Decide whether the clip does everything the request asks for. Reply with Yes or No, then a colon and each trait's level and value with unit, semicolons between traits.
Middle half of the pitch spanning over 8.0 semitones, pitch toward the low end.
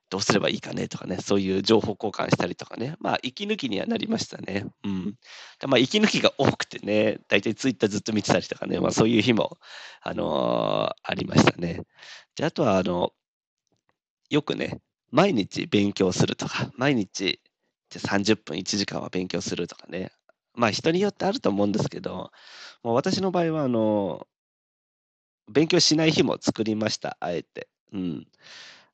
Yes: wide, 8.5 semitones; low, 110 Hz